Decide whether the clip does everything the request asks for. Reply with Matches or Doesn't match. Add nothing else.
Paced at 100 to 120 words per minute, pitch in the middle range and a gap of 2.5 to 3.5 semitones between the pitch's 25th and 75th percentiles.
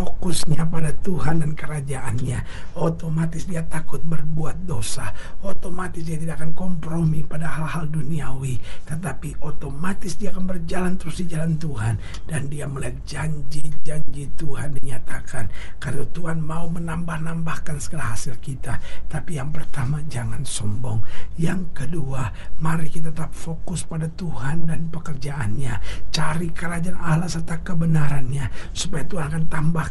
Doesn't match